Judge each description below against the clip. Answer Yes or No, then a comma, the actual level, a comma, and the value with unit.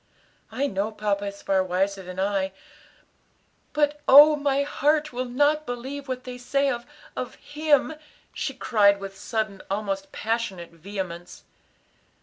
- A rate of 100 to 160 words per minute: Yes, slow, 135 wpm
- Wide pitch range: Yes, wide, 6.2 semitones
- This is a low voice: No, high, 225 Hz